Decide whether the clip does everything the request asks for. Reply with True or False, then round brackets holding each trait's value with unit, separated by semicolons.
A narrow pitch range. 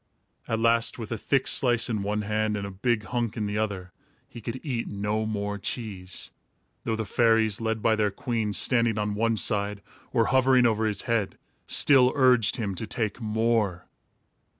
True (2.2 semitones)